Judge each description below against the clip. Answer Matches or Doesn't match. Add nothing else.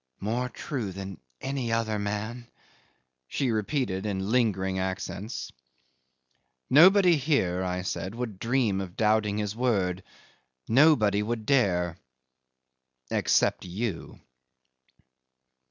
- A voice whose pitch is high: Doesn't match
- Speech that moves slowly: Matches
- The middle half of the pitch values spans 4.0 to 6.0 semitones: Matches